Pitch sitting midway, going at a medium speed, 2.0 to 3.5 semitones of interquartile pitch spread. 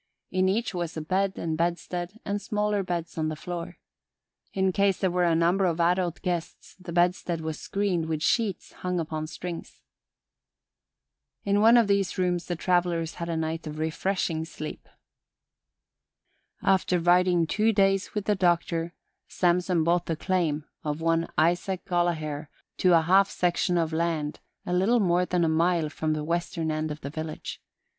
Yes: medium, 175 Hz; average, 165 wpm; narrow, 2.4 semitones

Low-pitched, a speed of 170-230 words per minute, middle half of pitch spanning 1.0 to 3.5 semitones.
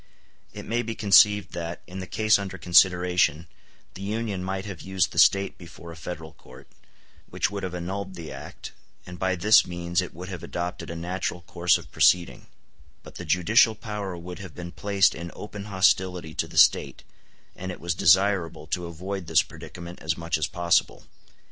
Yes: very low, 90 Hz; average, 185 wpm; narrow, 2.4 semitones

